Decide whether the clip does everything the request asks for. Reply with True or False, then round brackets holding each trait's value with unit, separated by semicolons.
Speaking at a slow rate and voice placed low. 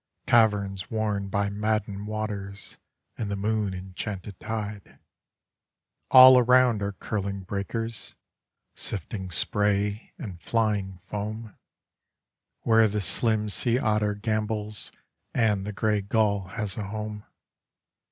True (110 wpm; 105 Hz)